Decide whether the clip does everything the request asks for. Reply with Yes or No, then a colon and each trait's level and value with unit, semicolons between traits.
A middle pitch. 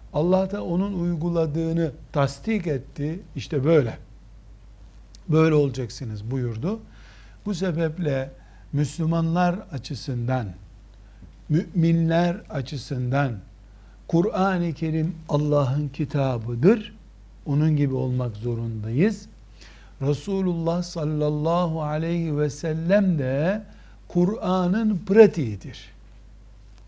Yes: medium, 150 Hz